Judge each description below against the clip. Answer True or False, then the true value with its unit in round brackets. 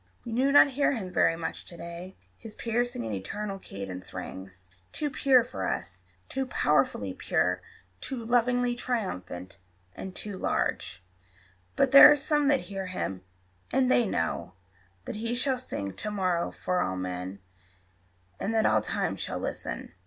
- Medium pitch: False (210 Hz)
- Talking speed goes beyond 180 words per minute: False (160 wpm)